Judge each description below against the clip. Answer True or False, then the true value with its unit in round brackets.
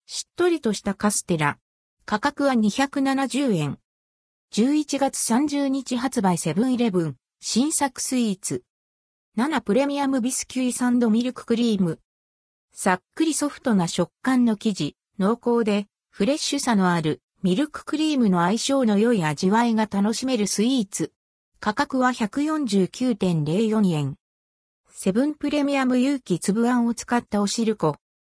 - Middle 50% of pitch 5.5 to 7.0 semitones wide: True (6.7 semitones)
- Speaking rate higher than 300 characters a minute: False (270 characters per minute)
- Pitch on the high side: True (225 Hz)